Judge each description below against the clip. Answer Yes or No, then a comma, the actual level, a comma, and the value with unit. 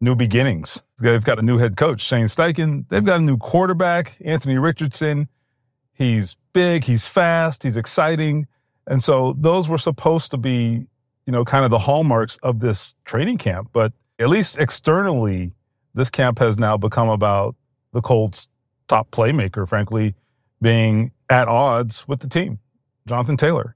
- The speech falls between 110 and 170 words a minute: Yes, average, 160 wpm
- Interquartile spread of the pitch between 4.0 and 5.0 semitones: Yes, average, 4.3 semitones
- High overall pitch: No, low, 125 Hz